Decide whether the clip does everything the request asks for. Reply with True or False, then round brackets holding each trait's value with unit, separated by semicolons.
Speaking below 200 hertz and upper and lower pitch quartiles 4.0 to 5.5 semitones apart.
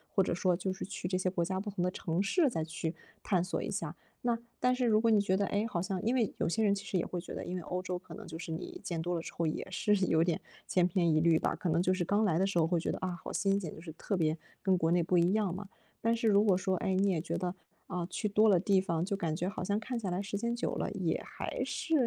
False (185 Hz; 2.9 semitones)